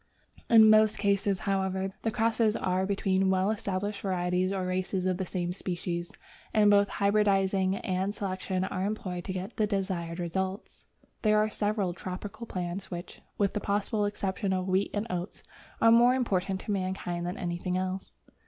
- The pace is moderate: Yes, average, 165 wpm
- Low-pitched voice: No, high, 190 Hz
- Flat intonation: Yes, narrow, 1.9 semitones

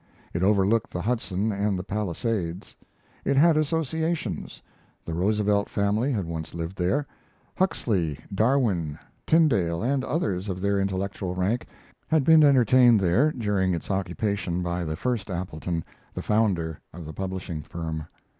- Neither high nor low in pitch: No, low, 100 Hz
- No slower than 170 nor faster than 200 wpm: No, average, 140 wpm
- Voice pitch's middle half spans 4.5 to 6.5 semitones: Yes, average, 5.2 semitones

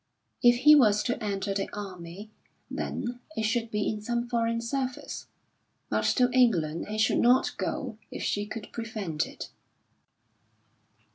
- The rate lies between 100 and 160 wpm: Yes, average, 145 wpm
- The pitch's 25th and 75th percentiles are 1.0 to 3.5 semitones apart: Yes, average, 2.9 semitones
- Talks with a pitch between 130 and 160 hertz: No, high, 225 Hz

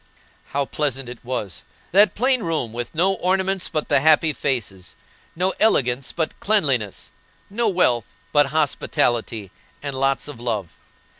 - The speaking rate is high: No, average, 140 wpm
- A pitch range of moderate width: No, wide, 6.8 semitones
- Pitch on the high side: No, medium, 140 Hz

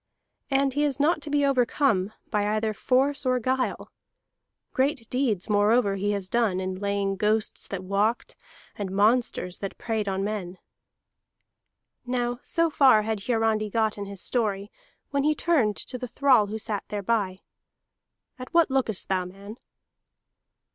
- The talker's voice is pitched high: Yes, high, 220 Hz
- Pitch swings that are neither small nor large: Yes, average, 4.2 semitones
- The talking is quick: No, average, 150 wpm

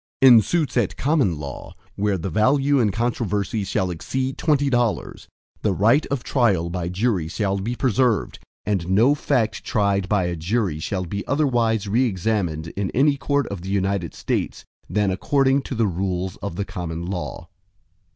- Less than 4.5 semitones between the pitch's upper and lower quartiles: No, average, 5.3 semitones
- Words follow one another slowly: No, average, 170 wpm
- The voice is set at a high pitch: No, low, 105 Hz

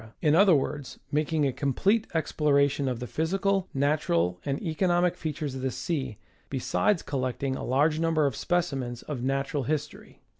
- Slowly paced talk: No, average, 160 wpm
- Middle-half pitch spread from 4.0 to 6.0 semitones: No, average, 3.5 semitones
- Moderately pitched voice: Yes, medium, 145 Hz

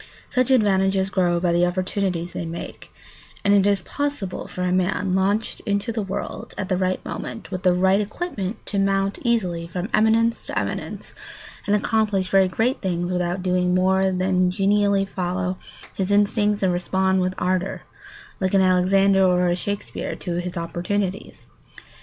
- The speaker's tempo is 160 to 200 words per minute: Yes, average, 165 wpm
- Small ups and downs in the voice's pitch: Yes, narrow, 1.9 semitones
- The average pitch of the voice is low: No, high, 190 Hz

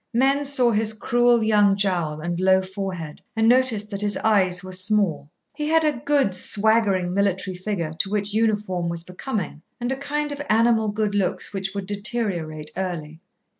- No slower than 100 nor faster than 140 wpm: No, average, 170 wpm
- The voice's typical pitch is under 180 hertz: No, high, 205 Hz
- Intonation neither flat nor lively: Yes, average, 3.7 semitones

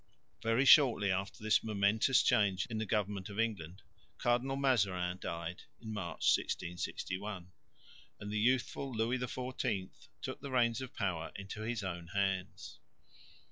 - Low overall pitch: Yes, low, 105 Hz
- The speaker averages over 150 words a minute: No, slow, 135 wpm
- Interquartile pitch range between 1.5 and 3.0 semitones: No, average, 4.2 semitones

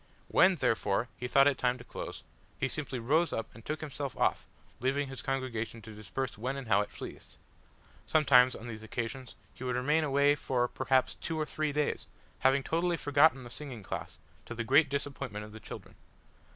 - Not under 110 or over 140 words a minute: No, average, 190 wpm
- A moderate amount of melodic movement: Yes, average, 3.4 semitones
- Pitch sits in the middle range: No, low, 130 Hz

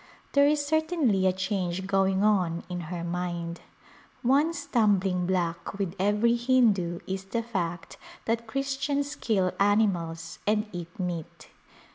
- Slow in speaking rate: Yes, slow, 130 wpm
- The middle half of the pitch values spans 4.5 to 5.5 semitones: Yes, average, 5.0 semitones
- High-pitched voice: Yes, high, 195 Hz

